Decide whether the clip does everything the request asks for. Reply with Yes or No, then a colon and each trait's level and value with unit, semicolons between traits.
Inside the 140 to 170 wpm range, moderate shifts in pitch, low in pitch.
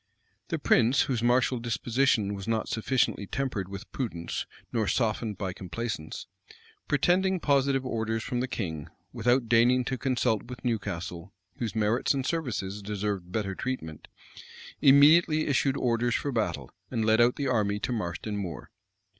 Yes: average, 150 wpm; average, 4.0 semitones; low, 115 Hz